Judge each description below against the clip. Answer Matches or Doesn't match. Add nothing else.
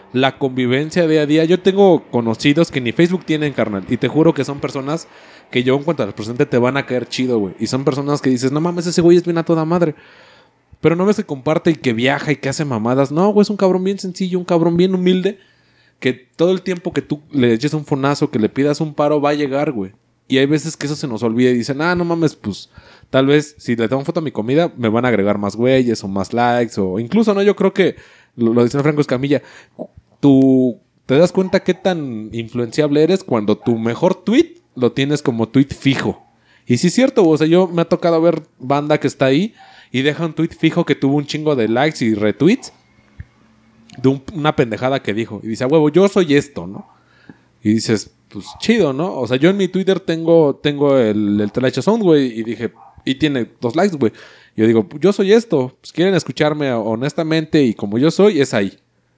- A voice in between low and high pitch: Matches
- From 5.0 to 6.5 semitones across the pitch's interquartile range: Matches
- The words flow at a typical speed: Doesn't match